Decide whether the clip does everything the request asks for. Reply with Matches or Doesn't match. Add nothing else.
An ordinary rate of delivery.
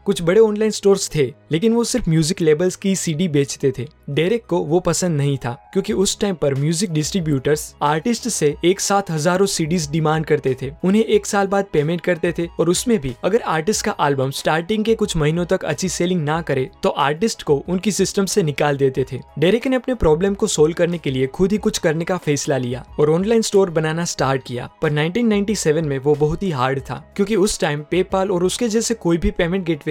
Doesn't match